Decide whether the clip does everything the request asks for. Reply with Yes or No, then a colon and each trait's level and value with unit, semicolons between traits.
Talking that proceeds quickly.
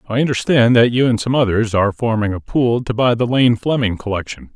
Yes: fast, 225 wpm